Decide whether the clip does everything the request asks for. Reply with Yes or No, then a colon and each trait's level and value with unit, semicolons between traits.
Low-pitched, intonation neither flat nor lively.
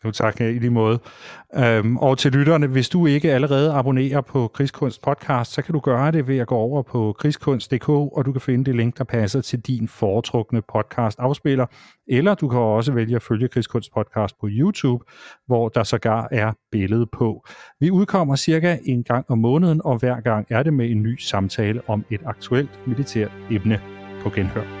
Yes: low, 125 Hz; average, 3.8 semitones